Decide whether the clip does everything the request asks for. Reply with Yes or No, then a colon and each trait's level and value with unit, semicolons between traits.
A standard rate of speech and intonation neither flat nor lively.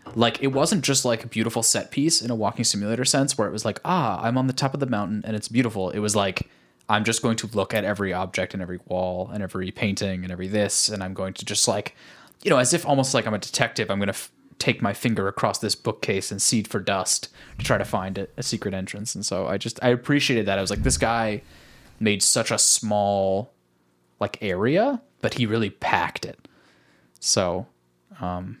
No: fast, 235 wpm; average, 3.8 semitones